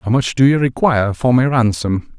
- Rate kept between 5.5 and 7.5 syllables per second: No, 5.2 syllables/s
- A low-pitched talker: Yes, low, 120 Hz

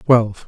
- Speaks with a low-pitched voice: Yes, low, 115 Hz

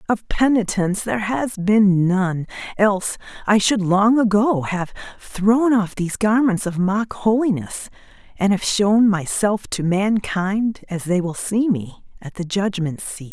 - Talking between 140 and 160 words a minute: Yes, average, 155 wpm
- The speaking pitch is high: Yes, high, 200 Hz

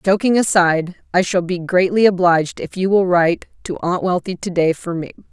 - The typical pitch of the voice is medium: Yes, medium, 180 Hz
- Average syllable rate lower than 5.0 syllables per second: No, 5.5 syllables/s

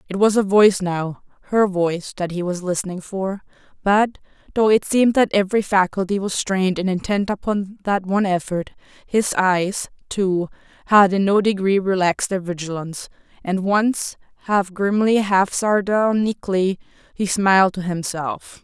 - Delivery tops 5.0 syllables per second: No, 4.8 syllables/s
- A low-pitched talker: No, high, 195 Hz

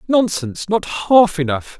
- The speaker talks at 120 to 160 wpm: Yes, slow, 135 wpm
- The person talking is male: Yes, male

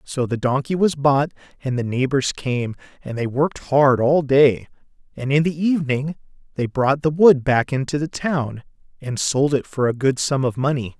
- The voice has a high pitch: No, low, 135 Hz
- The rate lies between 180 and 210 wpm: Yes, average, 195 wpm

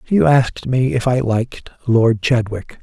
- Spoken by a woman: No, male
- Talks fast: No, average, 170 wpm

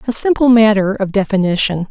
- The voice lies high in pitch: Yes, high, 210 Hz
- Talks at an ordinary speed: Yes, average, 155 wpm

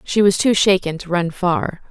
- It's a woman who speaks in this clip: Yes, female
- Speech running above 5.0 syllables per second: No, 4.6 syllables/s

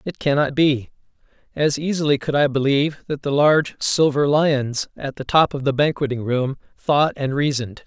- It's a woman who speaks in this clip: No, male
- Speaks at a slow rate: No, average, 170 wpm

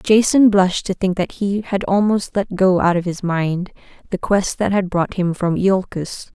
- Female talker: Yes, female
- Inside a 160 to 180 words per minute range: No, fast, 205 wpm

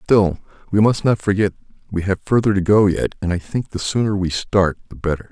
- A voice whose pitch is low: Yes, low, 100 Hz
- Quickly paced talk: Yes, fast, 225 wpm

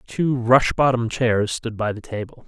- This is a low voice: Yes, low, 120 Hz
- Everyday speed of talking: Yes, average, 195 wpm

